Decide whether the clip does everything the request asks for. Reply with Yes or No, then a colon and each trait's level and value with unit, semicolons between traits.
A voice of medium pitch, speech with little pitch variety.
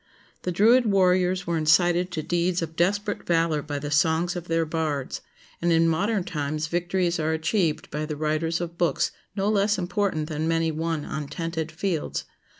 Yes: medium, 165 Hz; narrow, 2.3 semitones